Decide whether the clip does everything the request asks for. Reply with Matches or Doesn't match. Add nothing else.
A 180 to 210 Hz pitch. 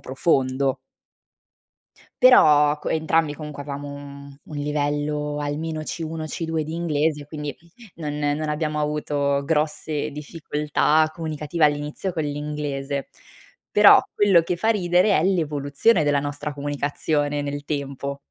Doesn't match